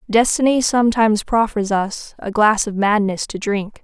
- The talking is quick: No, average, 155 wpm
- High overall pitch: Yes, high, 215 Hz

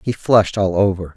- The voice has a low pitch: Yes, low, 100 Hz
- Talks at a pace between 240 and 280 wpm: No, fast, 205 wpm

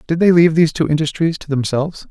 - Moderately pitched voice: Yes, medium, 160 Hz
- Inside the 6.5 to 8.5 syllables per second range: Yes, 7.1 syllables/s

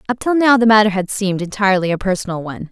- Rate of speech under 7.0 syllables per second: No, 7.5 syllables/s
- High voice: Yes, high, 200 Hz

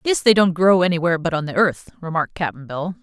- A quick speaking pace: Yes, fast, 240 wpm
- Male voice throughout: No, female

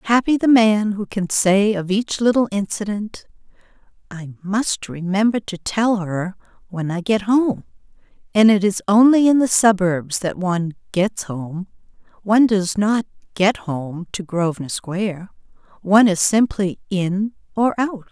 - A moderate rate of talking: Yes, average, 150 wpm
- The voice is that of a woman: Yes, female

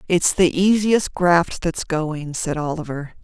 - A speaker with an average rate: Yes, average, 150 wpm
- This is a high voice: No, medium, 170 Hz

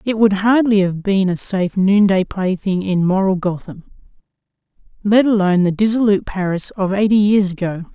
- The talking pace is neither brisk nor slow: Yes, average, 160 wpm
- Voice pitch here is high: Yes, high, 195 Hz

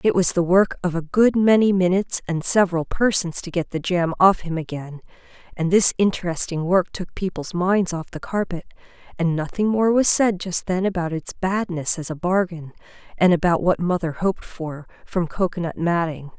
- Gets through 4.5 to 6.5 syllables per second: Yes, 5.1 syllables/s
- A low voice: No, medium, 180 Hz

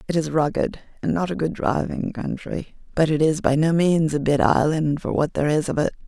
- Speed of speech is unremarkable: No, fast, 235 wpm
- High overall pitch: No, medium, 155 Hz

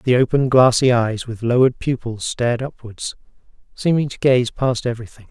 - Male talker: Yes, male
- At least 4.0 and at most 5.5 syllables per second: Yes, 5.3 syllables/s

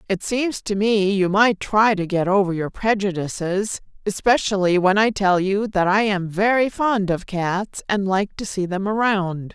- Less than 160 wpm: No, average, 190 wpm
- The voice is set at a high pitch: Yes, high, 200 Hz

